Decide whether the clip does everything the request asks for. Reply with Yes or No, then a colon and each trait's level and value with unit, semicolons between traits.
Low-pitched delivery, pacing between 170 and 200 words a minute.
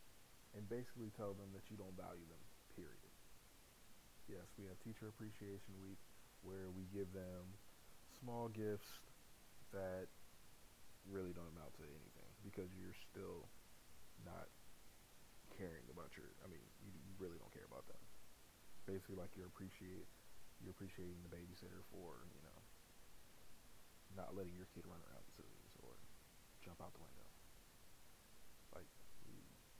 No: very low, 95 Hz; slow, 135 wpm